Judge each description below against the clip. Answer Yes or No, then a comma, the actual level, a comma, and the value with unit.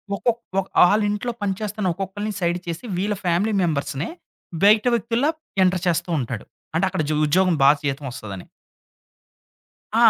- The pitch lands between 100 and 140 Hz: No, medium, 185 Hz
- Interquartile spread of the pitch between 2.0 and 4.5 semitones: No, average, 5.0 semitones